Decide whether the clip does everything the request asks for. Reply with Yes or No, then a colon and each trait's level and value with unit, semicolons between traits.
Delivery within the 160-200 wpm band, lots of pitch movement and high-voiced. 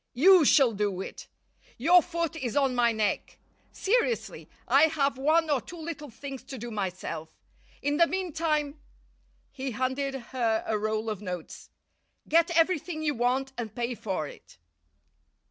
No: average, 150 wpm; wide, 5.7 semitones; very high, 270 Hz